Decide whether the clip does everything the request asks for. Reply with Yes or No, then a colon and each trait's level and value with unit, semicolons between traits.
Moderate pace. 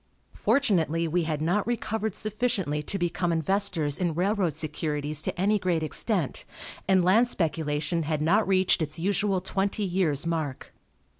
Yes: average, 145 wpm